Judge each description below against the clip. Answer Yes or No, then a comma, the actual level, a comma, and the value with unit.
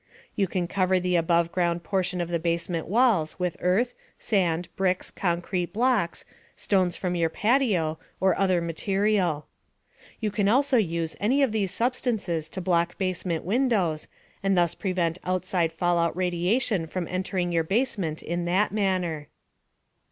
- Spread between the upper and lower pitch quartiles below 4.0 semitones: Yes, average, 2.8 semitones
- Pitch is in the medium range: Yes, medium, 180 Hz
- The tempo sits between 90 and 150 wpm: Yes, average, 145 wpm